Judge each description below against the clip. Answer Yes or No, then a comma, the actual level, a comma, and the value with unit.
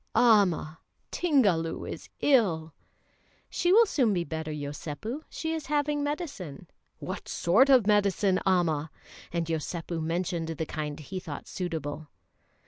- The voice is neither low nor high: Yes, medium, 175 Hz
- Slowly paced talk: Yes, slow, 130 wpm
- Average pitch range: No, wide, 7.6 semitones